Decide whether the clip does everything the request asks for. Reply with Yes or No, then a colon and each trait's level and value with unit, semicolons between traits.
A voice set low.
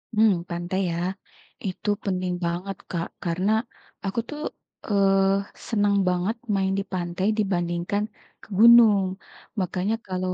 No: high, 190 Hz